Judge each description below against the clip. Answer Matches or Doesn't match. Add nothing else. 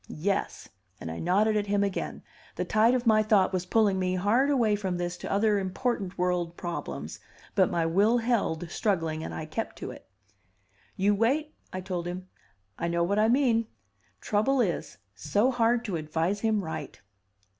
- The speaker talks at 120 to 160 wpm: Doesn't match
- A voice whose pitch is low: Doesn't match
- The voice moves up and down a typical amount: Matches